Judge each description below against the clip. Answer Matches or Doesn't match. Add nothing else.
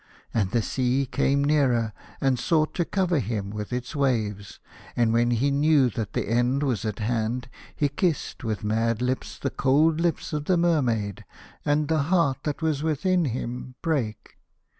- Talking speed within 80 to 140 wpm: Doesn't match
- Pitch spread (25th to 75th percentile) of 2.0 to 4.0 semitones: Doesn't match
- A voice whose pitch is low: Matches